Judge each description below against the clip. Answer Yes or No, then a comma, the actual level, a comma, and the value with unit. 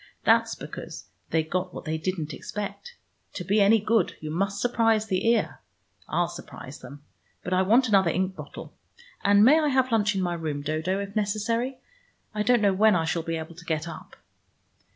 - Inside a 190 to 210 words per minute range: Yes, average, 195 wpm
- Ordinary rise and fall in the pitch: Yes, average, 4.6 semitones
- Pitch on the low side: No, high, 195 Hz